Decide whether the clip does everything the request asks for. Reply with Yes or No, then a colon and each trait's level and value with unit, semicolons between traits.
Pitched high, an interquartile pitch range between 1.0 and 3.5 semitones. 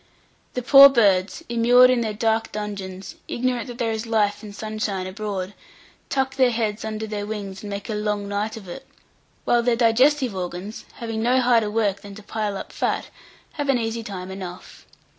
Yes: high, 215 Hz; average, 2.7 semitones